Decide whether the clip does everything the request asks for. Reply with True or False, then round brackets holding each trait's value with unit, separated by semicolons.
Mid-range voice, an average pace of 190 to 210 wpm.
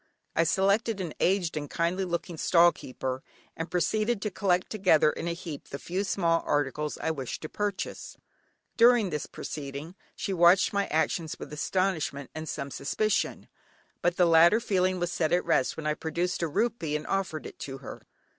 False (170 Hz; 180 wpm)